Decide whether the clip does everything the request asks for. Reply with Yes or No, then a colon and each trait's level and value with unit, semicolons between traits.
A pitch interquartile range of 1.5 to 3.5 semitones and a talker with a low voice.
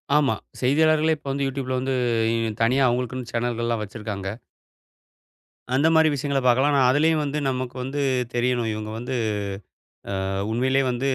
Yes: average, 2.7 semitones; low, 130 Hz